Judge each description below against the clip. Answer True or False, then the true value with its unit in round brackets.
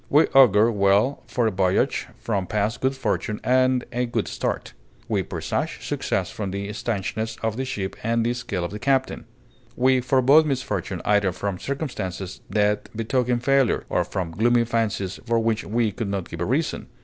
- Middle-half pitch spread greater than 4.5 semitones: False (4.1 semitones)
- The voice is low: True (115 Hz)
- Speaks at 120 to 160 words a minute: False (175 wpm)